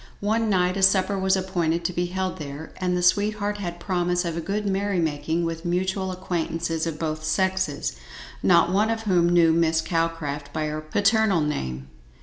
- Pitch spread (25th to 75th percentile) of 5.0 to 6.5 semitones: No, average, 2.8 semitones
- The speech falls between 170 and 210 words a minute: Yes, average, 180 wpm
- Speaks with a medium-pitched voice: Yes, medium, 175 Hz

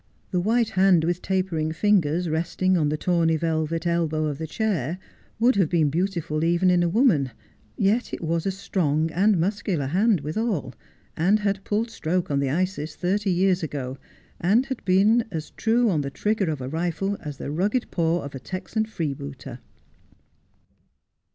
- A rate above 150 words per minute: Yes, average, 170 wpm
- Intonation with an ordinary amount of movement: Yes, average, 4.2 semitones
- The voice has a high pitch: No, medium, 175 Hz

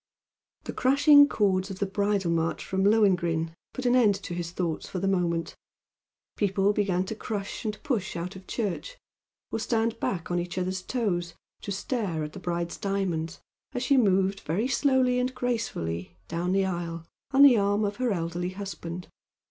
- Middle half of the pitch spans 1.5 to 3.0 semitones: No, average, 4.3 semitones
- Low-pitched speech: No, high, 195 Hz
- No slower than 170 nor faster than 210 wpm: Yes, average, 175 wpm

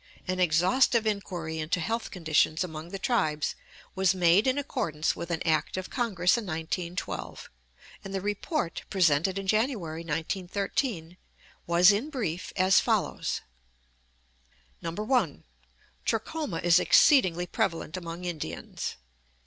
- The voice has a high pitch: No, medium, 180 Hz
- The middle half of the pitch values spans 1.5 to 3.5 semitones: No, average, 4.0 semitones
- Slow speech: Yes, slow, 120 wpm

